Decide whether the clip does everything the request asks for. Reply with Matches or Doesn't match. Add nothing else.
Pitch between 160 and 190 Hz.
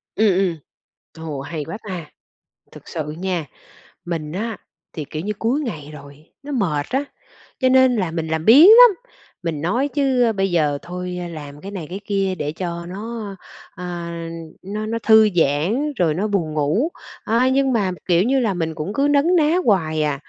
Matches